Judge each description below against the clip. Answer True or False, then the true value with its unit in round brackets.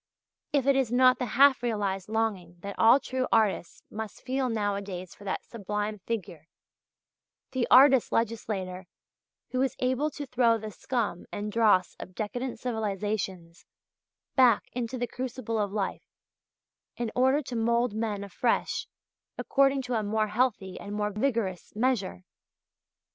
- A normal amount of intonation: True (3.8 semitones)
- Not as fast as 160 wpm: True (145 wpm)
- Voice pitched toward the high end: True (225 Hz)